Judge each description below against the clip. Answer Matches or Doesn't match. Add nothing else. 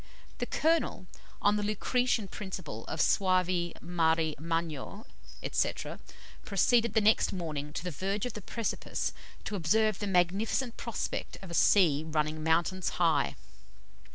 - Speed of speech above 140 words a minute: Doesn't match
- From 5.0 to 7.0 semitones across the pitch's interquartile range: Doesn't match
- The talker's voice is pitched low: Doesn't match